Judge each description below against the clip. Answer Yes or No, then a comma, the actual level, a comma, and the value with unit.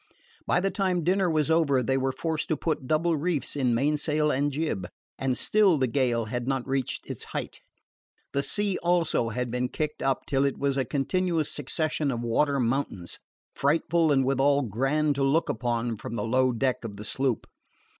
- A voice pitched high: No, medium, 140 Hz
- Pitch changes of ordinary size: Yes, average, 3.9 semitones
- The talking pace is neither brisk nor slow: Yes, average, 185 wpm